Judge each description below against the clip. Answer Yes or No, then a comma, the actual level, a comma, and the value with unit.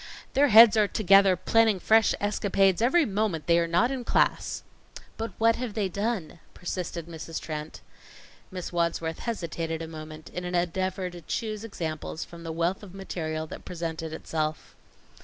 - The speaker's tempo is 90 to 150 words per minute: No, average, 160 wpm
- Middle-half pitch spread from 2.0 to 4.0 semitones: No, average, 4.5 semitones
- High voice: No, medium, 180 Hz